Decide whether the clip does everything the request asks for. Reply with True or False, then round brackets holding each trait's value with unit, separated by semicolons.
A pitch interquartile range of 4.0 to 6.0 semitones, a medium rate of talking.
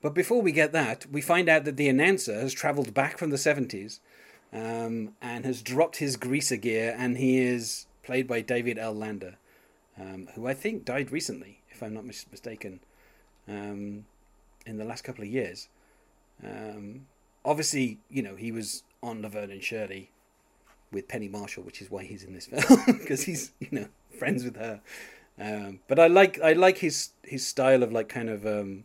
True (4.9 semitones; 185 wpm)